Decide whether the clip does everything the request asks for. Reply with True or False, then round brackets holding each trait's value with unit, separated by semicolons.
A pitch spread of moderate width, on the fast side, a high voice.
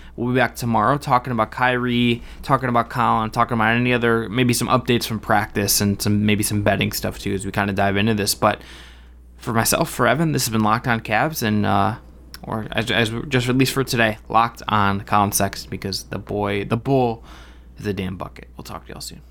False (3.2 semitones; 220 wpm; 110 Hz)